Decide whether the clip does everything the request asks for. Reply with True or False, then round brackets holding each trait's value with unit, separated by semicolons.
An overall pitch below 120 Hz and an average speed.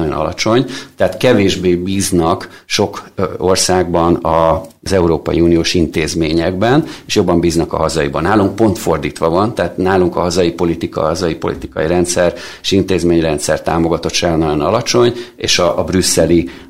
True (90 Hz; 130 wpm)